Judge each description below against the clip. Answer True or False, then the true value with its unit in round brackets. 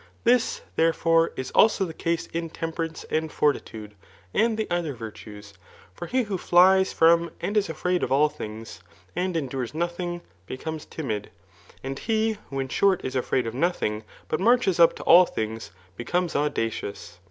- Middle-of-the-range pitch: True (165 Hz)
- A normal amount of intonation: False (5.7 semitones)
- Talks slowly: False (165 wpm)